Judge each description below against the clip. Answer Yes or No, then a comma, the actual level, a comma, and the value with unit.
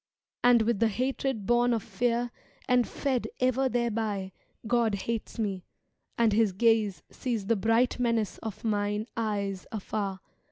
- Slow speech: No, average, 145 wpm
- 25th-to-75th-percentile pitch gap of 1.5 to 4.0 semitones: Yes, narrow, 2.6 semitones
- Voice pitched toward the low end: No, high, 225 Hz